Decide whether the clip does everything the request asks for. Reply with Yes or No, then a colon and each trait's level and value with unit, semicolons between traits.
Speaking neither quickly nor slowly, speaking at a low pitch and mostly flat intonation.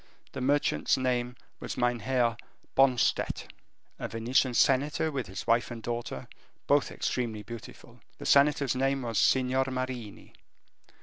No: slow, 125 wpm; low, 125 Hz; narrow, 2.2 semitones